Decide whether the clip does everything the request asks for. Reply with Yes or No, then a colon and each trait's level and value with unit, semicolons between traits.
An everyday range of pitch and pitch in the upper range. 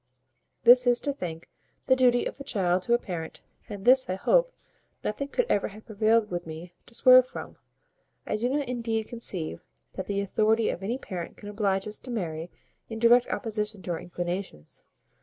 Yes: average, 4.8 semitones; high, 215 Hz